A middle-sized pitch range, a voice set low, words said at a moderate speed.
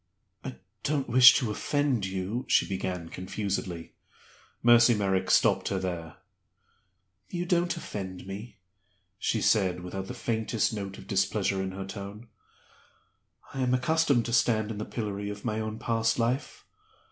Yes: average, 4.1 semitones; low, 110 Hz; average, 150 wpm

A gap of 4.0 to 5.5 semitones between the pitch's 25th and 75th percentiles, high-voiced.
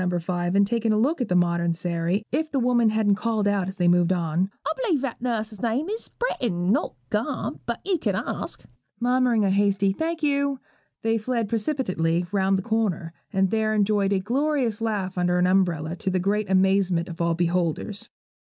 Yes: average, 4.7 semitones; high, 200 Hz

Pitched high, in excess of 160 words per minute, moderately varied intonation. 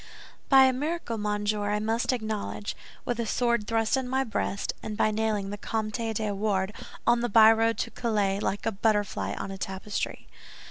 No: high, 215 Hz; average, 180 wpm; narrow, 2.1 semitones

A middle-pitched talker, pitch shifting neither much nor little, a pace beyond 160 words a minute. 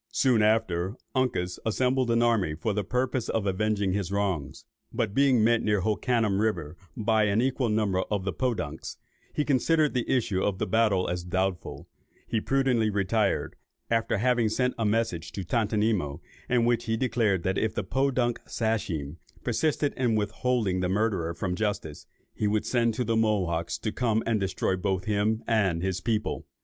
No: low, 110 Hz; average, 3.7 semitones; average, 170 wpm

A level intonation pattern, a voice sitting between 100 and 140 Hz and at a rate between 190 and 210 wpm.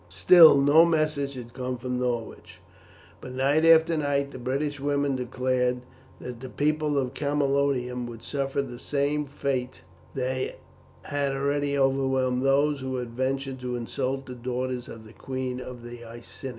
No: narrow, 2.1 semitones; low, 135 Hz; average, 155 wpm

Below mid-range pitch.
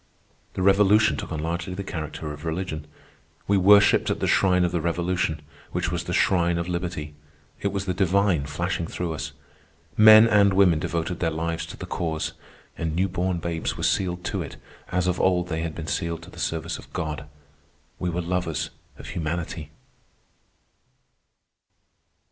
Yes: very low, 85 Hz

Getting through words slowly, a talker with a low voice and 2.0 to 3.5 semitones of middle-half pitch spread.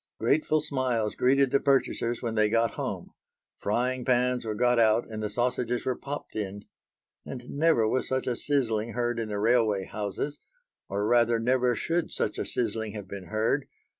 No: average, 175 wpm; low, 120 Hz; average, 2.9 semitones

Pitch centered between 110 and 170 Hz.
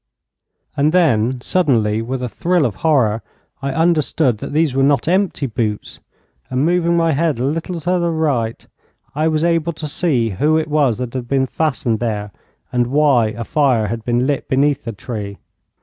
Yes: medium, 140 Hz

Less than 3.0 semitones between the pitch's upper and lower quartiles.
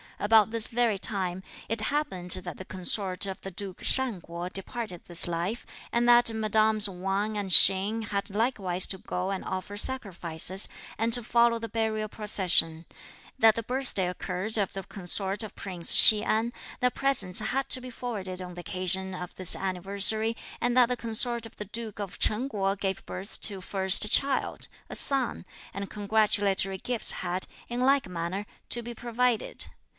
No: average, 3.5 semitones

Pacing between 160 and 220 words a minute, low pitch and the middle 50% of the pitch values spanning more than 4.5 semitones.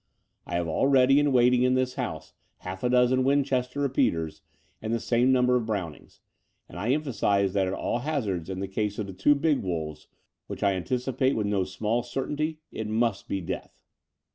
Yes: average, 190 wpm; low, 120 Hz; average, 5.1 semitones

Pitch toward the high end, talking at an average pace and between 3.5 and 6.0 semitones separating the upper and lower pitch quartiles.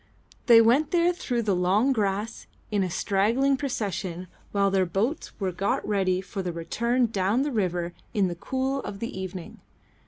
Yes: high, 205 Hz; average, 175 wpm; average, 4.5 semitones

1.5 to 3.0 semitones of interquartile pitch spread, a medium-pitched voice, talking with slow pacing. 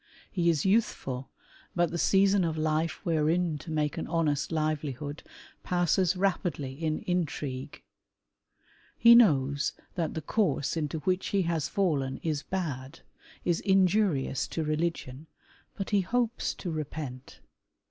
No: average, 3.7 semitones; medium, 160 Hz; slow, 130 wpm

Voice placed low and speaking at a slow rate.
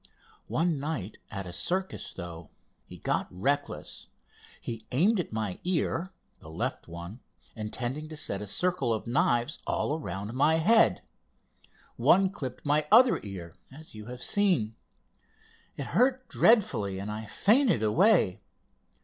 Yes: low, 130 Hz; slow, 130 wpm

